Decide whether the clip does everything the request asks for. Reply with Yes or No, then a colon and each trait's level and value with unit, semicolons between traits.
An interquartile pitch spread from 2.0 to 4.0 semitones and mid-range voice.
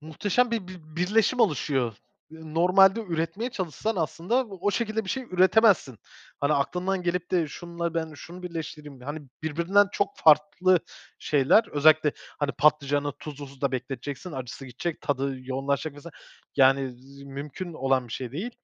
No: average, 4.9 semitones; medium, 160 Hz